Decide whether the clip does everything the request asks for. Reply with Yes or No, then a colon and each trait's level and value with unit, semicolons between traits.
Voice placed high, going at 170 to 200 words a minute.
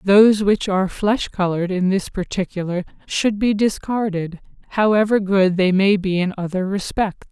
No: high, 195 Hz; average, 155 wpm